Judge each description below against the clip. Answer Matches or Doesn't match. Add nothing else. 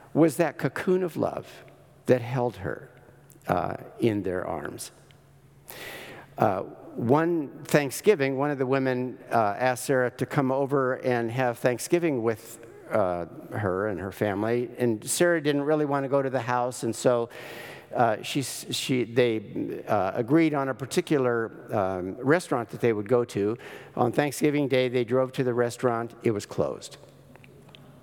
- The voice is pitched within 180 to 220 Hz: Doesn't match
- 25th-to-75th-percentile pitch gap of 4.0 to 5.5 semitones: Doesn't match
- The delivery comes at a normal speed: Matches